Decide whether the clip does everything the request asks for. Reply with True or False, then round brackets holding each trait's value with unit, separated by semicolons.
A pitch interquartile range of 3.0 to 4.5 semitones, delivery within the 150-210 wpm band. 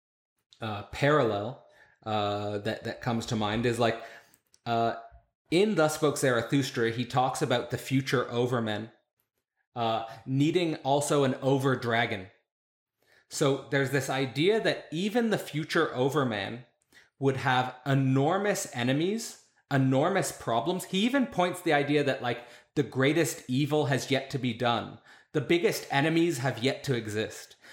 False (4.1 semitones; 140 wpm)